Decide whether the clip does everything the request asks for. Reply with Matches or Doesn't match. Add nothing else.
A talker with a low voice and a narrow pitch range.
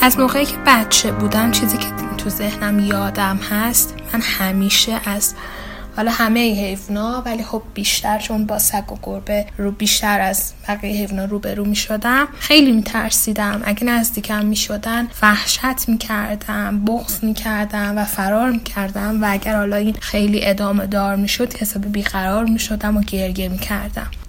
Doesn't match